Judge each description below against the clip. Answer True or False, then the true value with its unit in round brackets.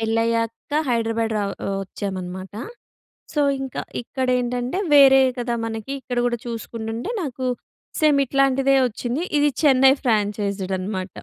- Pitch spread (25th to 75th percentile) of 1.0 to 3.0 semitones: False (3.5 semitones)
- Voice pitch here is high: True (235 Hz)